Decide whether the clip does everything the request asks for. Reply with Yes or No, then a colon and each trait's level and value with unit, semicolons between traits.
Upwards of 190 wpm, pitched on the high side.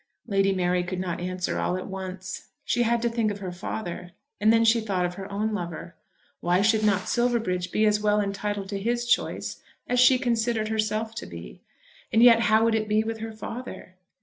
Yes: fast, 205 wpm; high, 210 Hz